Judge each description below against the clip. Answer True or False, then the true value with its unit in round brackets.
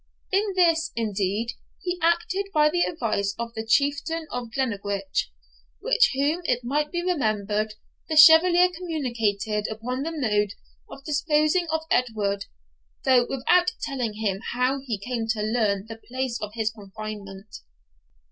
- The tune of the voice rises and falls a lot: True (6.7 semitones)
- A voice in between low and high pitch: False (245 Hz)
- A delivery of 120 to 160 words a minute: True (140 wpm)